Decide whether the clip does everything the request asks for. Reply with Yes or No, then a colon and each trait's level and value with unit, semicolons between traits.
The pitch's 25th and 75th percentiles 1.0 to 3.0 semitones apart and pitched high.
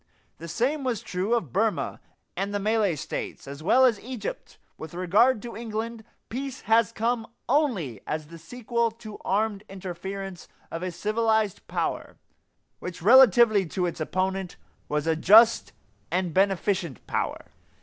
No: average, 4.5 semitones; high, 205 Hz